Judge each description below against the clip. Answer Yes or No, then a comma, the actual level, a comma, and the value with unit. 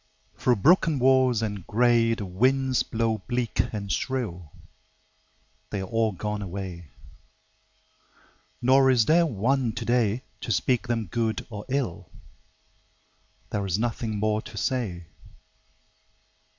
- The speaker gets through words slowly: Yes, slow, 120 wpm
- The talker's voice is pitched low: Yes, low, 115 Hz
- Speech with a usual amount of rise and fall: Yes, average, 3.6 semitones